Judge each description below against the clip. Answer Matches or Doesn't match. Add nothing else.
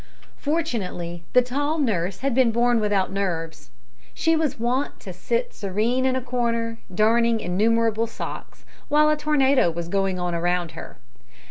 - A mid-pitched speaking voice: Doesn't match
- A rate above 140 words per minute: Matches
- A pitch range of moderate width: Doesn't match